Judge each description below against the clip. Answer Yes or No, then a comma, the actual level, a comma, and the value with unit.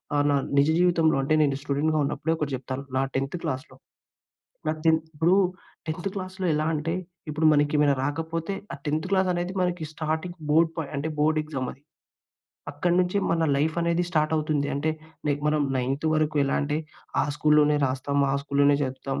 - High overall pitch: No, medium, 155 Hz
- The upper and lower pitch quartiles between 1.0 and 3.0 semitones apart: Yes, narrow, 2.4 semitones